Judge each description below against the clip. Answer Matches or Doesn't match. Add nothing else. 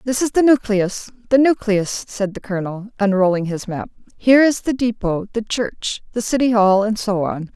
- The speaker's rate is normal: Matches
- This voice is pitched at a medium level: Doesn't match